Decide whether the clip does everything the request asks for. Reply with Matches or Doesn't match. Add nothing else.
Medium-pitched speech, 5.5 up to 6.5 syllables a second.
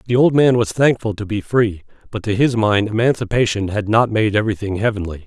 Doesn't match